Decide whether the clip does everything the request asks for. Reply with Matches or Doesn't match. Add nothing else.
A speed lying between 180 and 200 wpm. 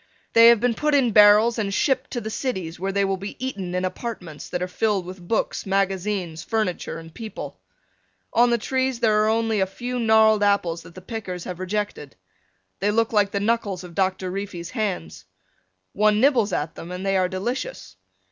Matches